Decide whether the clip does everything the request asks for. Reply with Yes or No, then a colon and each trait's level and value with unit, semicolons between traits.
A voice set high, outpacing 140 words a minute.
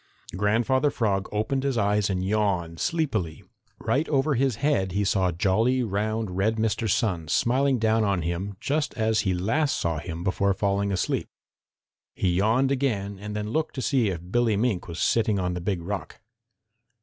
No: low, 105 Hz; average, 175 wpm